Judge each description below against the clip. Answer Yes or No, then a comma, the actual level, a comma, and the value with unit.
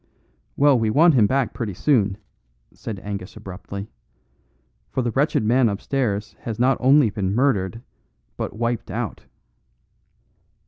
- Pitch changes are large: No, average, 4.5 semitones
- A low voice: Yes, low, 115 Hz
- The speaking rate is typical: No, slow, 130 wpm